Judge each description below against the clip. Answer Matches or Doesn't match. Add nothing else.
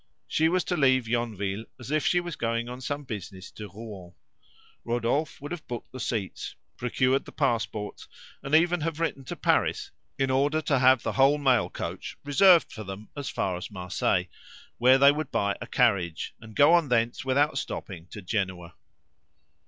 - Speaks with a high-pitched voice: Doesn't match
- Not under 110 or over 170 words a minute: Doesn't match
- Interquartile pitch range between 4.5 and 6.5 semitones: Matches